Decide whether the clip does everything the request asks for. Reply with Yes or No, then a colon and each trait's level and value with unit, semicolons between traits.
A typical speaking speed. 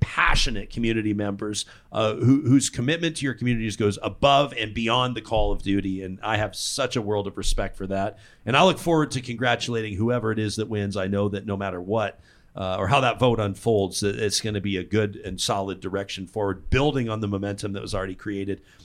No: fast, 225 wpm